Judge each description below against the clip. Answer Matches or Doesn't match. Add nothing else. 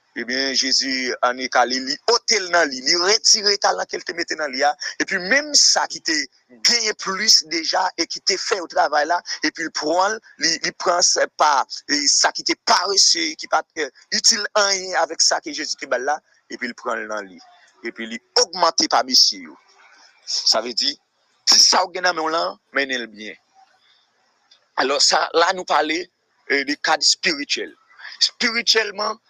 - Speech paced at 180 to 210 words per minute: Matches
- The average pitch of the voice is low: Doesn't match